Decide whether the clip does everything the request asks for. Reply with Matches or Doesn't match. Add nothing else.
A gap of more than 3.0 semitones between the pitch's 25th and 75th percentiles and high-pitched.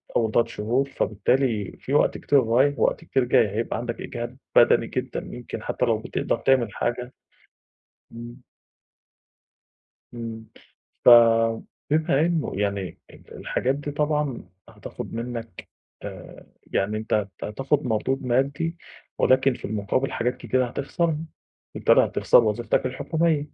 Doesn't match